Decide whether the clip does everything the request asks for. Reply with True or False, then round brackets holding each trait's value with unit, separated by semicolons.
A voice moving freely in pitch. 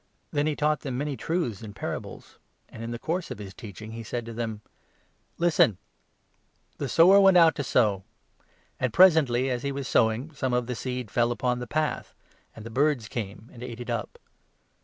False (4.6 semitones)